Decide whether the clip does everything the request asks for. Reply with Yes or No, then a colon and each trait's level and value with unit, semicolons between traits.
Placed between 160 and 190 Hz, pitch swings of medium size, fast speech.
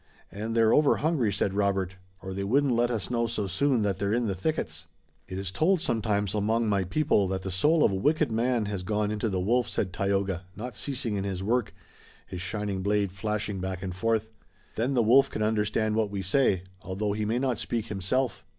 No: low, 105 Hz; average, 3.3 semitones; fast, 215 wpm